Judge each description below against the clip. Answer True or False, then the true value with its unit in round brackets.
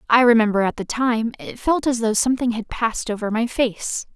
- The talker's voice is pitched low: False (230 Hz)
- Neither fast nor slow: False (215 wpm)